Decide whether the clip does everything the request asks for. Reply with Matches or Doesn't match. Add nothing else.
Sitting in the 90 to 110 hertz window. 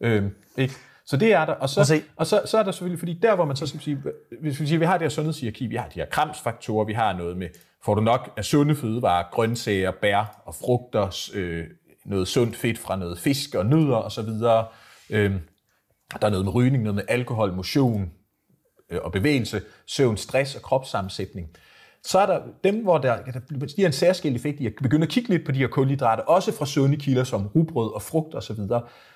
Doesn't match